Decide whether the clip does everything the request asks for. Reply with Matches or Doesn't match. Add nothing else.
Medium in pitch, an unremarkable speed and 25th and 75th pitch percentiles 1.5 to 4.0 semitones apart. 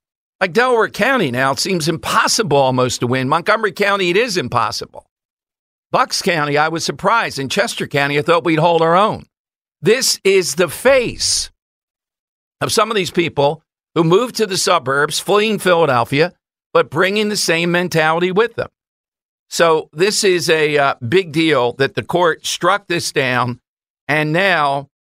Doesn't match